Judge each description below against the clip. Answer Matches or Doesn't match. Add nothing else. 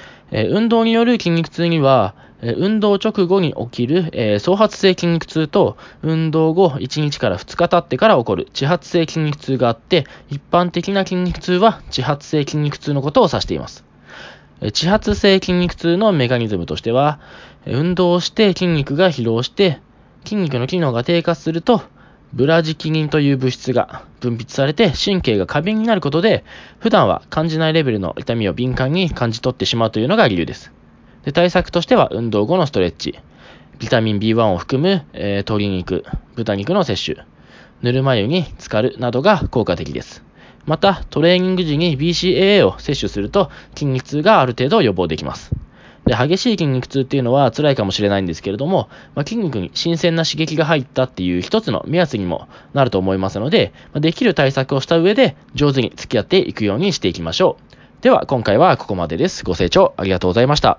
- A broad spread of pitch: Matches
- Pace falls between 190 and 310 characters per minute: Doesn't match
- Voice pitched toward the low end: Doesn't match